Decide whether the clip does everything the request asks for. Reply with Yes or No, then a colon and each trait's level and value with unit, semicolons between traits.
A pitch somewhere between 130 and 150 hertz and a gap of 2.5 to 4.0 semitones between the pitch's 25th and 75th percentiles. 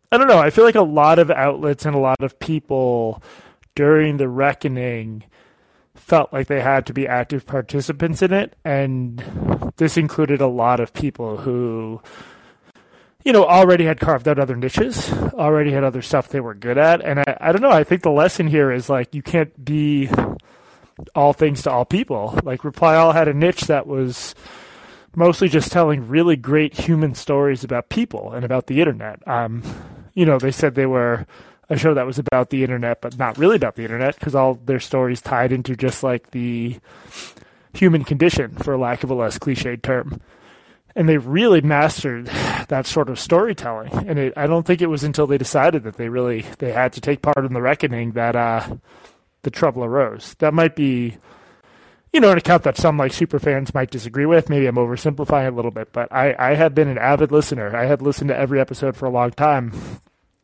Yes: medium, 140 Hz; average, 3.6 semitones